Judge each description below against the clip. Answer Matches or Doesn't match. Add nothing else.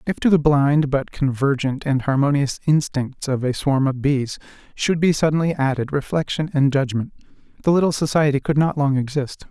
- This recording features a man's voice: Matches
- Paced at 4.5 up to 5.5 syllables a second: Matches